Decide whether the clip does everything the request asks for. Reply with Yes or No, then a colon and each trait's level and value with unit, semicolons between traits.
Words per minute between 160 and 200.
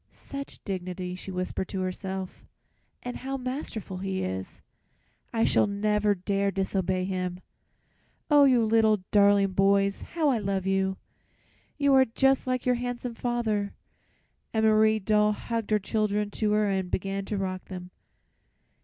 No: average, 145 wpm